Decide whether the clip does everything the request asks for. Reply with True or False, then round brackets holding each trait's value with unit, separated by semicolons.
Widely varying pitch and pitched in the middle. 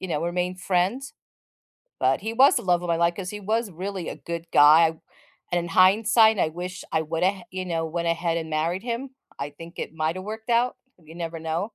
False (3.4 semitones; 175 Hz)